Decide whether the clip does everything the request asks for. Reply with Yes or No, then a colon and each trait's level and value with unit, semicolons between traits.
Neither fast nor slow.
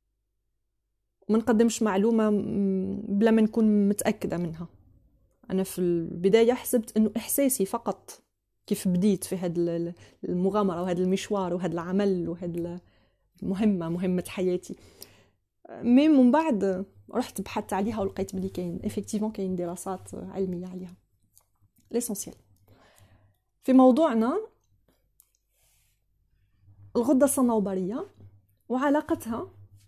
Yes: average, 95 wpm